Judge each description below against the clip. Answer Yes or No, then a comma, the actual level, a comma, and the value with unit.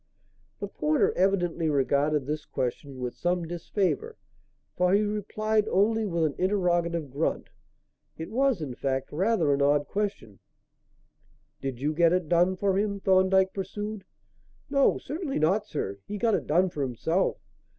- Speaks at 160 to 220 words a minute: No, average, 150 wpm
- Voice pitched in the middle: Yes, medium, 180 Hz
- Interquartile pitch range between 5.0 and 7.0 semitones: Yes, average, 5.3 semitones